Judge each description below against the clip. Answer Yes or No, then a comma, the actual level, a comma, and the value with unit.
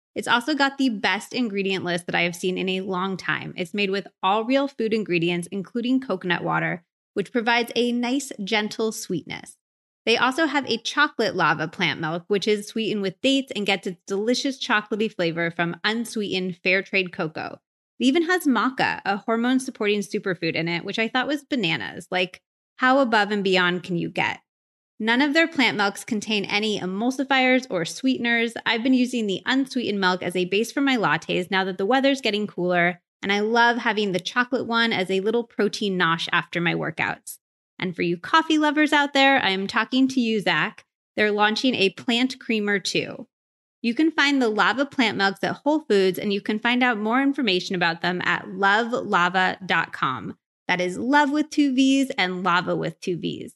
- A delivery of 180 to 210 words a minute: Yes, average, 195 wpm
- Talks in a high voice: Yes, high, 210 Hz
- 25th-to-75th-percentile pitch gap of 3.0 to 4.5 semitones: No, wide, 5.4 semitones